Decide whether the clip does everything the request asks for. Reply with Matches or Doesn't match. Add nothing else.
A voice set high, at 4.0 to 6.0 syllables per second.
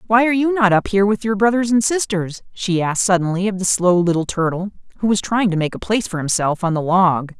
Doesn't match